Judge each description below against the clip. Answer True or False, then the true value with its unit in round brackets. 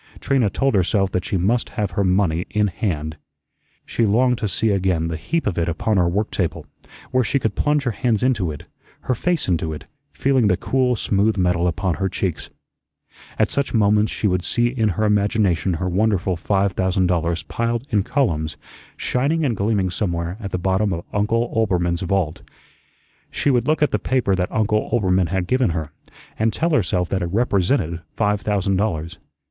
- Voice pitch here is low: True (100 Hz)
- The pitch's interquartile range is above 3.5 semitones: True (4.4 semitones)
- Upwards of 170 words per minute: True (190 wpm)